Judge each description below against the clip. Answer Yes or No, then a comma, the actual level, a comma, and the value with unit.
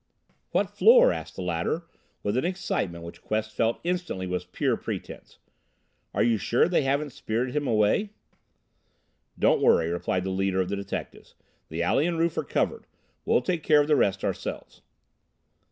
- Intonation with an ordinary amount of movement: No, wide, 8.5 semitones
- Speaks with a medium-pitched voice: No, low, 110 Hz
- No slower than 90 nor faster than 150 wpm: No, average, 170 wpm